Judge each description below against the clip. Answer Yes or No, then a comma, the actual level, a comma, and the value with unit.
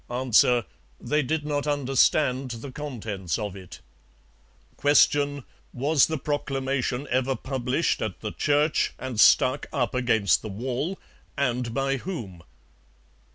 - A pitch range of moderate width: Yes, average, 3.3 semitones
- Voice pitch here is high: No, low, 130 Hz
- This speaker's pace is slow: Yes, slow, 120 wpm